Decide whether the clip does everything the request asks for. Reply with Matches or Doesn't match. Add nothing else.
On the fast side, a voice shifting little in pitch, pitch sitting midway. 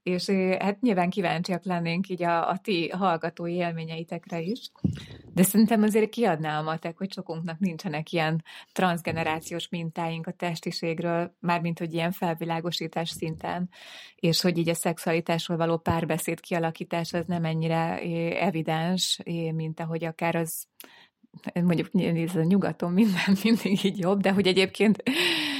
Doesn't match